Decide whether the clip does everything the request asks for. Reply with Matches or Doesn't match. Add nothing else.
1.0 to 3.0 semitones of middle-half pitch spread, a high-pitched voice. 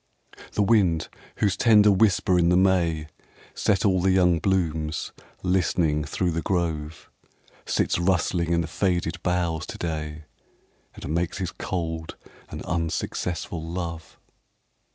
Doesn't match